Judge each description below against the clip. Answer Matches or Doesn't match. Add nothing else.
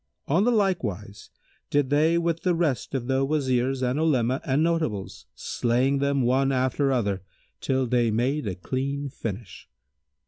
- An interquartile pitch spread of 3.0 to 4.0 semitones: Matches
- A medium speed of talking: Matches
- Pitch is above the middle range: Doesn't match